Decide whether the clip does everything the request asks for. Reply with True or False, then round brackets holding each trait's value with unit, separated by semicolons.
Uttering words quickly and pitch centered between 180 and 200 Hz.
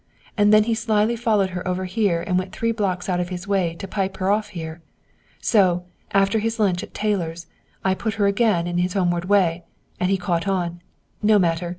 True (210 wpm; 190 Hz)